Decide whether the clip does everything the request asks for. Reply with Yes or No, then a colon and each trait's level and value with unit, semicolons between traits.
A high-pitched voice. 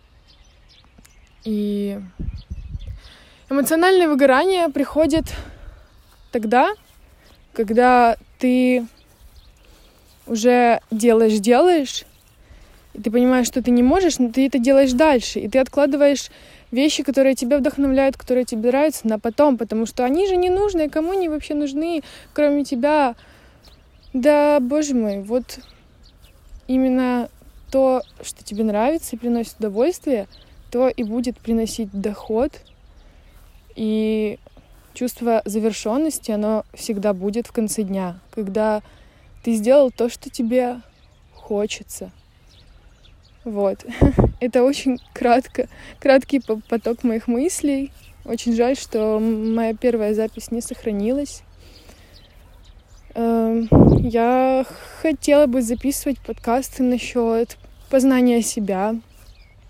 Yes: high, 245 Hz